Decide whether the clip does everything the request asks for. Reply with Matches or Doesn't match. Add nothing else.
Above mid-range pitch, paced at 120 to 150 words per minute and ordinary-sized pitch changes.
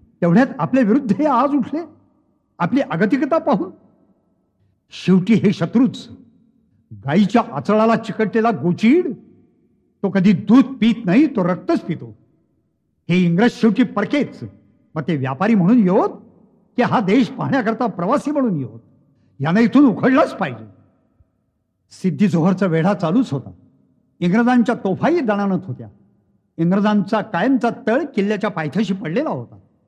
Doesn't match